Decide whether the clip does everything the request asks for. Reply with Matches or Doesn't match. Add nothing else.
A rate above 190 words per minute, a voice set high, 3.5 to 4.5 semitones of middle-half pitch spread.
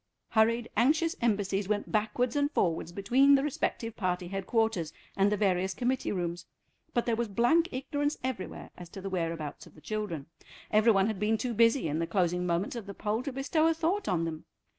Doesn't match